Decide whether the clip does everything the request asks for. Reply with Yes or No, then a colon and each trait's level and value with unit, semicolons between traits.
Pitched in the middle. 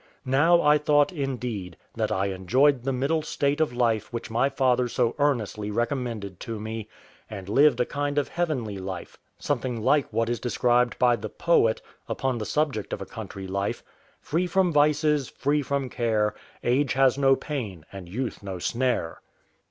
No: low, 125 Hz